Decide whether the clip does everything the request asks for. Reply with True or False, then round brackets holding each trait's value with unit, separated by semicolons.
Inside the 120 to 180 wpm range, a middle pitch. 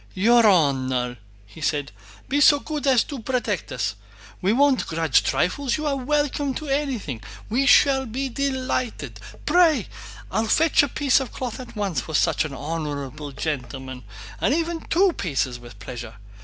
False (155 wpm; 230 Hz)